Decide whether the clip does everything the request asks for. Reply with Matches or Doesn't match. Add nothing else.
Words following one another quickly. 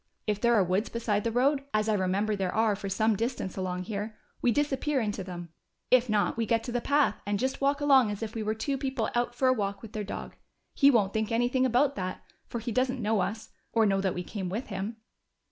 Matches